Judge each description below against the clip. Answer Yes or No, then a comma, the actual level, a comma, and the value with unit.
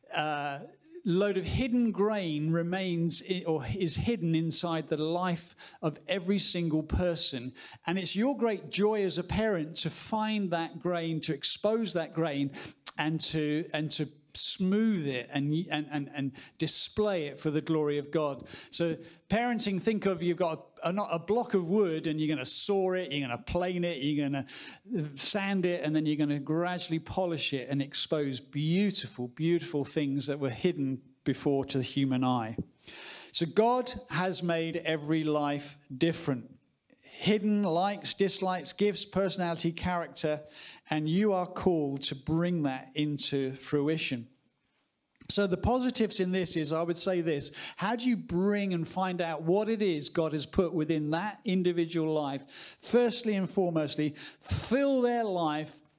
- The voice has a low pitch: No, medium, 165 Hz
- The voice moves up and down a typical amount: Yes, average, 4.0 semitones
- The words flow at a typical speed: Yes, average, 165 wpm